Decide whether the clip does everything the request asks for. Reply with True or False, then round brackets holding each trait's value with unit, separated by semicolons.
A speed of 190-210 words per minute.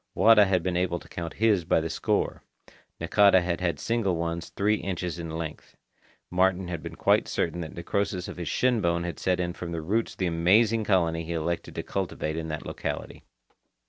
True (200 wpm)